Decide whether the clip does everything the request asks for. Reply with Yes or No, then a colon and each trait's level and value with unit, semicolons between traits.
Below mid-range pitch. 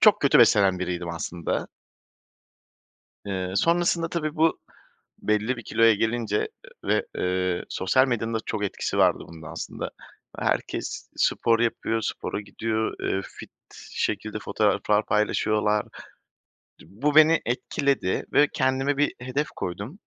Yes: low, 110 Hz